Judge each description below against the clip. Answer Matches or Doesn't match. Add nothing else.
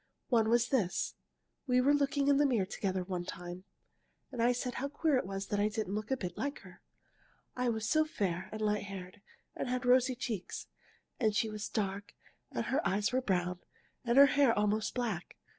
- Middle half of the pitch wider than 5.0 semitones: Doesn't match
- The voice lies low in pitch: Doesn't match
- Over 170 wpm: Matches